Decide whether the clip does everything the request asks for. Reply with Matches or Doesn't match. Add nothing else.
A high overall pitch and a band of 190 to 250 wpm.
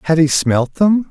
Doesn't match